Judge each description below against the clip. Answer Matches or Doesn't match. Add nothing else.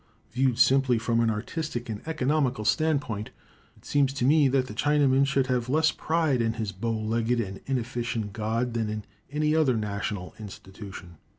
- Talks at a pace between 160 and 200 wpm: Matches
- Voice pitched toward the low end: Matches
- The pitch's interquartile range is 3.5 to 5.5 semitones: Matches